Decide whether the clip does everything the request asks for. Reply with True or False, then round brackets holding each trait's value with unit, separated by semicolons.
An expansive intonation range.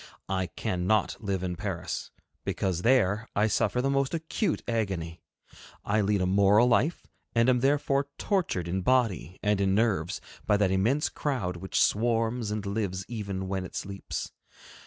False (4.3 semitones)